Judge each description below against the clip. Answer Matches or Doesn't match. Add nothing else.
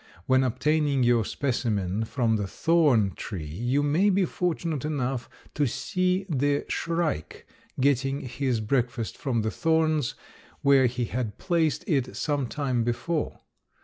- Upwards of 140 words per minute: Doesn't match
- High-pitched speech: Doesn't match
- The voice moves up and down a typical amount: Matches